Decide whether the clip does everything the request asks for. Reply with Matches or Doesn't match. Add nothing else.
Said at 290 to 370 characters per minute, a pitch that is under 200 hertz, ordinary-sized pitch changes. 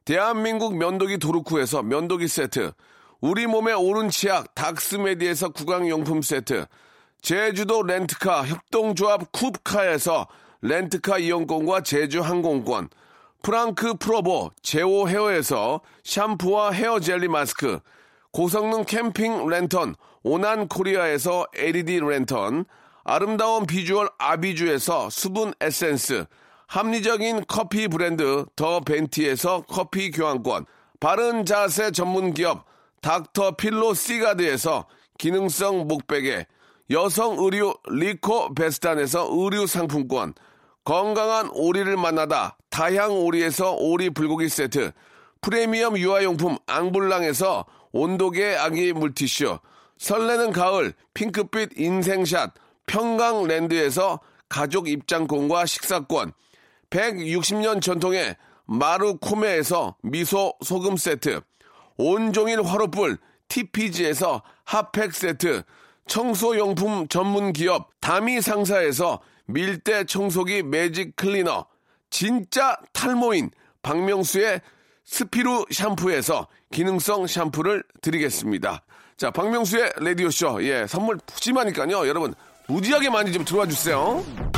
Doesn't match